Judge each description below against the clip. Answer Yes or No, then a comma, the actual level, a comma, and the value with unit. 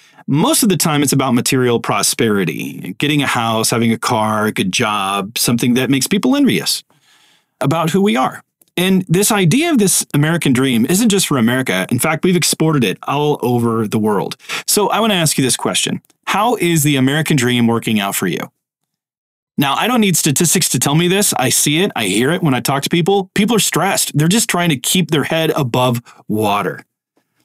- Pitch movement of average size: No, wide, 6.8 semitones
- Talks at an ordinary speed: No, fast, 210 wpm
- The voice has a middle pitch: Yes, medium, 150 Hz